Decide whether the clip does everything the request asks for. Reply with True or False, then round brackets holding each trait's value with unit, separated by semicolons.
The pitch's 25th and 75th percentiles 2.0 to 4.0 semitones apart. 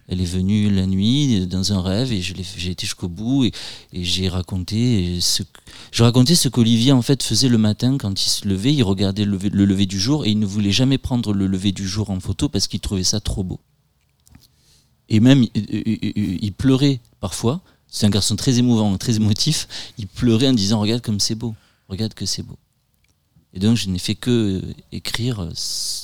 True (3.6 semitones)